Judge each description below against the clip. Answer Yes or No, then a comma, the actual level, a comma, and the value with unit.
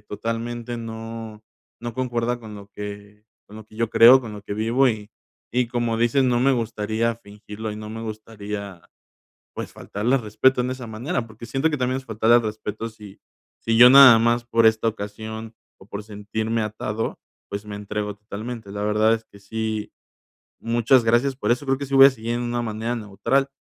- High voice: No, low, 115 Hz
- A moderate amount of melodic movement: No, narrow, 2.1 semitones